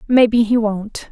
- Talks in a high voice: Yes, high, 225 Hz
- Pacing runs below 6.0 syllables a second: Yes, 4.2 syllables/s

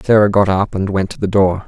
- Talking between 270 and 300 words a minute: Yes, fast, 285 wpm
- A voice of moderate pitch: No, low, 100 Hz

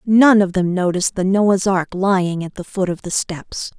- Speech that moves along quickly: Yes, fast, 220 wpm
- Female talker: Yes, female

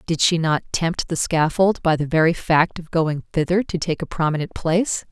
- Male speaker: No, female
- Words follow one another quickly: Yes, fast, 210 wpm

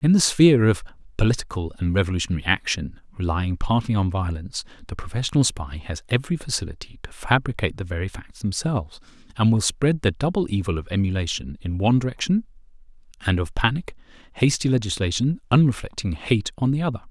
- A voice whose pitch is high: No, low, 110 Hz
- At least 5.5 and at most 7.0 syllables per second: Yes, 6.4 syllables/s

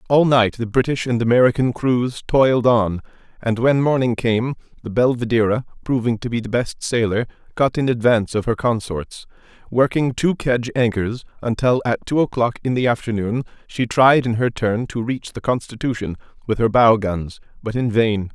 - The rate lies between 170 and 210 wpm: Yes, average, 175 wpm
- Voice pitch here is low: Yes, low, 120 Hz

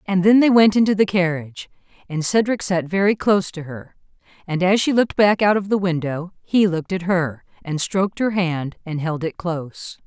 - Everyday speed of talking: No, fast, 210 wpm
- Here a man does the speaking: No, female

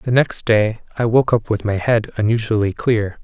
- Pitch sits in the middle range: No, low, 110 Hz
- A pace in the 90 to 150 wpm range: No, fast, 205 wpm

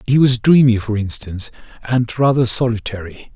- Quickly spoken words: No, average, 145 wpm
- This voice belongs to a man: Yes, male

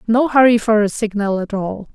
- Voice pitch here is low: No, high, 215 Hz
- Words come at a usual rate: No, fast, 215 wpm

